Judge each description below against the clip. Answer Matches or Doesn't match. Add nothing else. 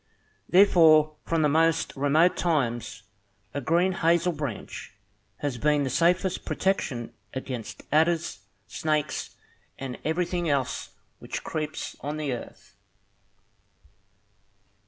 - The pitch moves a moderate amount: Matches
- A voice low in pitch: Doesn't match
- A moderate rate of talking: Doesn't match